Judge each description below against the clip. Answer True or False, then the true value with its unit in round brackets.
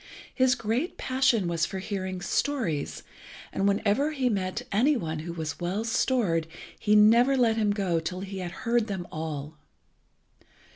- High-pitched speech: True (200 Hz)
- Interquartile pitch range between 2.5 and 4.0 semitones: False (5.5 semitones)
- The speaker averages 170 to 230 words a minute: False (155 wpm)